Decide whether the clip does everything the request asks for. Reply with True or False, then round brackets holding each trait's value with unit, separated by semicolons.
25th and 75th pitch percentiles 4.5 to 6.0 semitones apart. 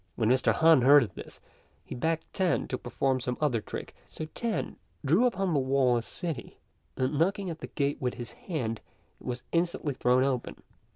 True (4.9 semitones)